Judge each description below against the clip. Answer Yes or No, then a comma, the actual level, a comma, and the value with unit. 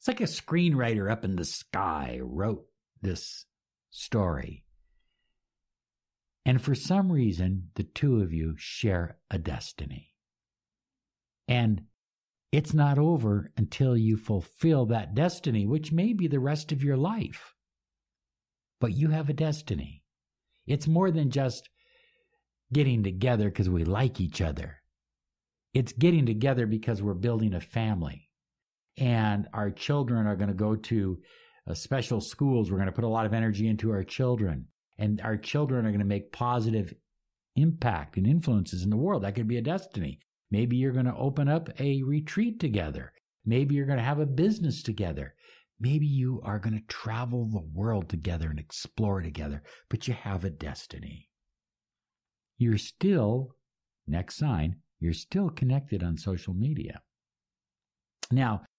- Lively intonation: Yes, wide, 6.0 semitones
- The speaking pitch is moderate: No, low, 115 Hz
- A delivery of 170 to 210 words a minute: No, average, 150 wpm